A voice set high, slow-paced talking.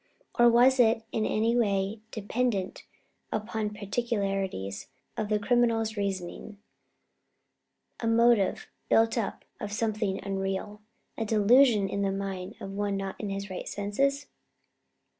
Yes: high, 210 Hz; slow, 125 wpm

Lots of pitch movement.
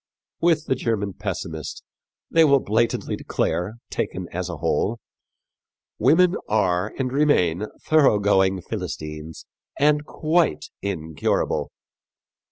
Yes: wide, 8.8 semitones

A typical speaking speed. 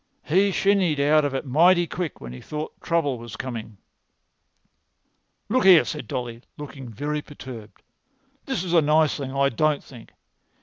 Yes: average, 160 wpm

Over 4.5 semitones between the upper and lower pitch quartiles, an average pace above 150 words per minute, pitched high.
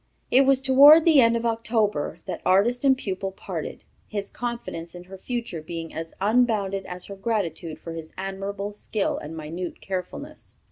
Yes: average, 5.0 semitones; average, 170 wpm; high, 200 Hz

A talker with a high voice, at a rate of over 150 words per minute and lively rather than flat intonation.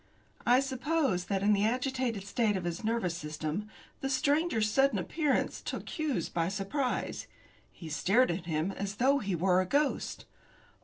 Yes: high, 210 Hz; average, 160 wpm; wide, 6.5 semitones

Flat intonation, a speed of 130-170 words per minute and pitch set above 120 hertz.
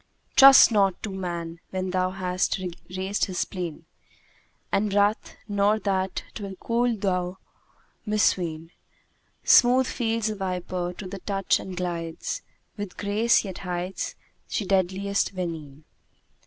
Yes: narrow, 2.3 semitones; slow, 135 wpm; high, 190 Hz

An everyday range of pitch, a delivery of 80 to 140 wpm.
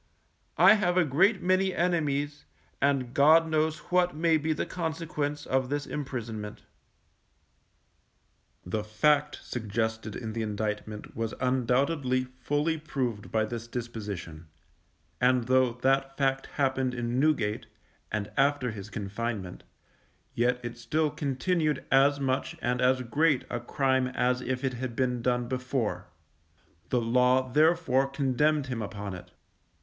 Yes: average, 3.9 semitones; slow, 135 wpm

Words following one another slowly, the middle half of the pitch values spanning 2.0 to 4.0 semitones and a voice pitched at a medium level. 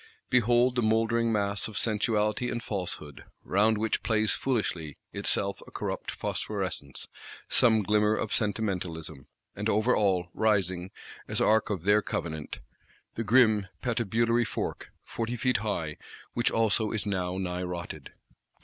No: slow, 130 wpm; average, 3.4 semitones; low, 105 Hz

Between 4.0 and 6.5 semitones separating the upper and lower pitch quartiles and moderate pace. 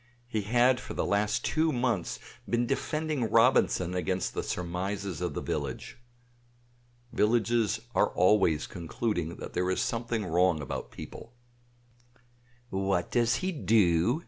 No: average, 5.0 semitones; slow, 125 wpm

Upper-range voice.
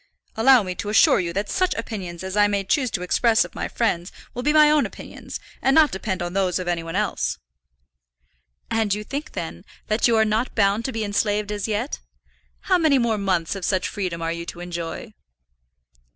Yes: high, 205 Hz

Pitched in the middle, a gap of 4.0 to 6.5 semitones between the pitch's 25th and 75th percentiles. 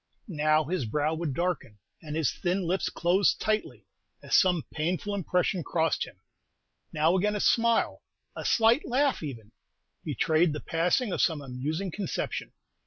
Yes: medium, 170 Hz; average, 4.3 semitones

